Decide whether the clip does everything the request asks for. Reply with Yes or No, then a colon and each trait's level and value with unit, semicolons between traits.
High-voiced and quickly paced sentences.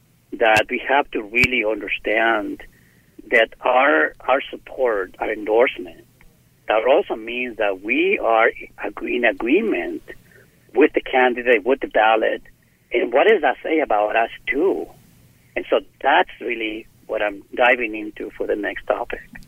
No: very high, 340 Hz; average, 140 wpm